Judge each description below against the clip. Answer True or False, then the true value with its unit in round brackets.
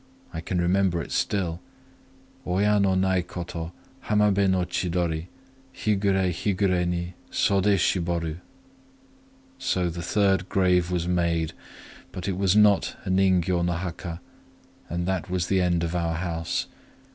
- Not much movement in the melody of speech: True (2.0 semitones)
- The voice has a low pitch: True (90 Hz)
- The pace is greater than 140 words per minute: False (135 wpm)